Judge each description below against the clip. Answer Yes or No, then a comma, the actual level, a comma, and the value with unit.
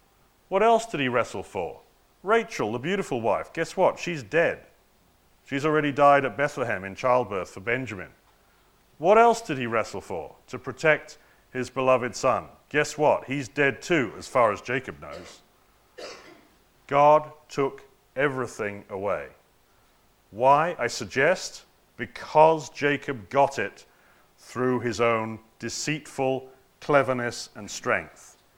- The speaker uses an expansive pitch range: No, average, 3.6 semitones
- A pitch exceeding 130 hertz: Yes, medium, 140 Hz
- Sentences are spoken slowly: Yes, slow, 130 wpm